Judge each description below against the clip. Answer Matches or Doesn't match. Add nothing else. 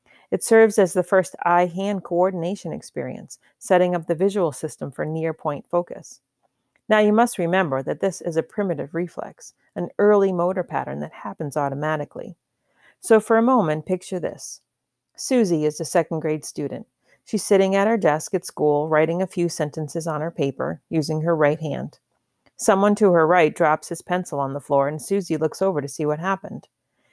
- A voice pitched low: Doesn't match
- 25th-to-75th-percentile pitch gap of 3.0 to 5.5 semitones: Matches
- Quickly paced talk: Doesn't match